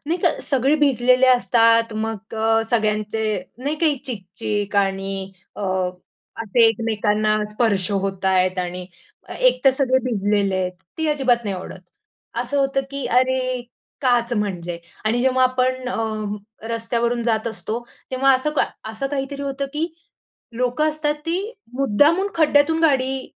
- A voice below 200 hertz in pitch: No, high, 235 Hz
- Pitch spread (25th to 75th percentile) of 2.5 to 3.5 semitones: No, average, 4.3 semitones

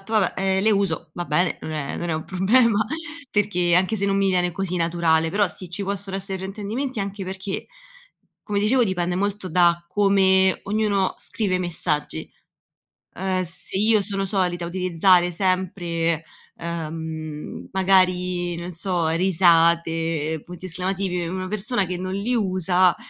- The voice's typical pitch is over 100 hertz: Yes, medium, 185 Hz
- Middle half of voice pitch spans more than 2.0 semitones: Yes, narrow, 2.4 semitones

